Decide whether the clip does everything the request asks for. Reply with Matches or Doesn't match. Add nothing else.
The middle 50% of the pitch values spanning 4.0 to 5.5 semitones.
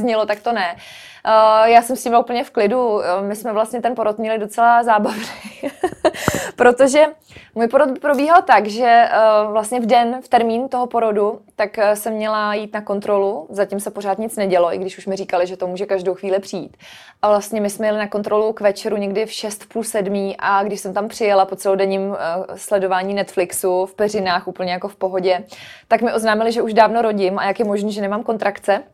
Doesn't match